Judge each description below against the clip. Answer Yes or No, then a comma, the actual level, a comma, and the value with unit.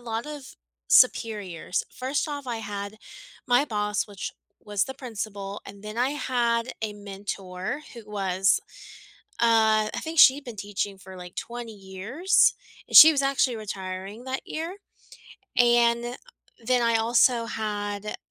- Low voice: No, high, 225 Hz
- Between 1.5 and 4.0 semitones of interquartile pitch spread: Yes, average, 3.5 semitones